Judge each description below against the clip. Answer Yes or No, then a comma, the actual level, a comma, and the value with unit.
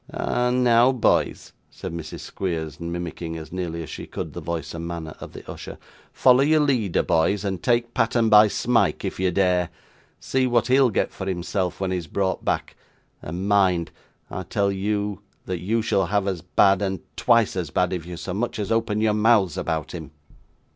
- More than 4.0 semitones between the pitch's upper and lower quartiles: Yes, average, 4.4 semitones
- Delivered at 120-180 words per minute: No, average, 195 wpm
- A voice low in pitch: Yes, very low, 95 Hz